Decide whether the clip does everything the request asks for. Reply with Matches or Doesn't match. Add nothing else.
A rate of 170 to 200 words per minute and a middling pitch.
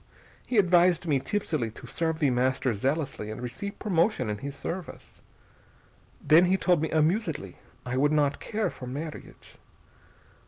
Doesn't match